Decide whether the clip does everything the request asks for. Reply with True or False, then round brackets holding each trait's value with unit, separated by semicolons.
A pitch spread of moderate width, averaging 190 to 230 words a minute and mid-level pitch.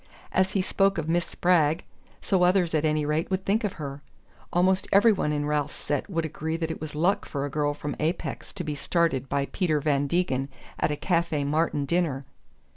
True (3.4 semitones; 205 wpm; 160 Hz)